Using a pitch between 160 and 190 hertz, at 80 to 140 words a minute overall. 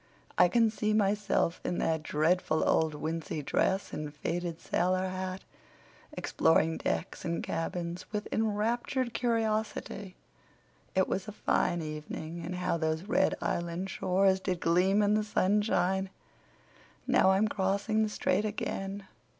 Yes: medium, 185 Hz; slow, 135 wpm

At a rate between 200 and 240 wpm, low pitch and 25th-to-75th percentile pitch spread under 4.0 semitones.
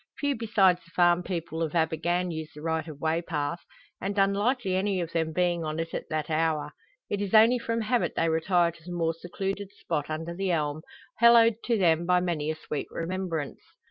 No: fast, 205 wpm; medium, 175 Hz; average, 3.3 semitones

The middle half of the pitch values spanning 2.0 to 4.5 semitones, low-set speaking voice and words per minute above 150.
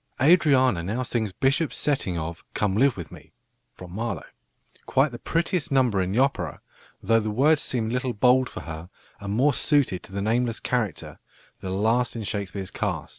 No: average, 5.0 semitones; low, 115 Hz; average, 180 wpm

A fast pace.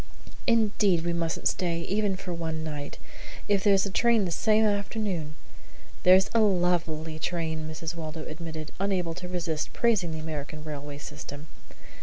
No: average, 155 wpm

